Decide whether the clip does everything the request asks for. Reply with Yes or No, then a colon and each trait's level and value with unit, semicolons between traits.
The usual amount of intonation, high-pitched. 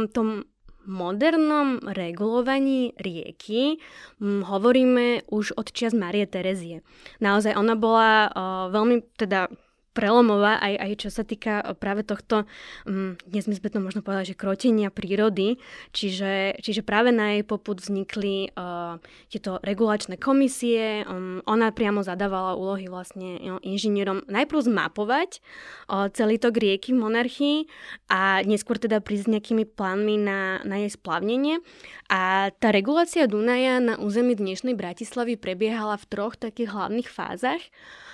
Yes: average, 3.3 semitones; high, 210 Hz